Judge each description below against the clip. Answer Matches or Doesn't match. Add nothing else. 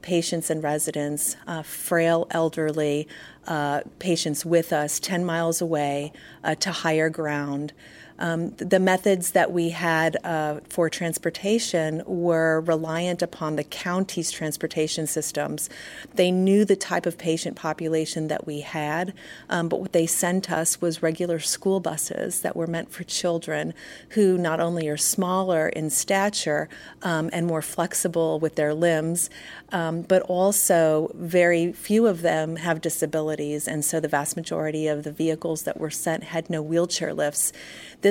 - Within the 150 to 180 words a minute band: Matches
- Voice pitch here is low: Doesn't match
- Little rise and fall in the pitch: Matches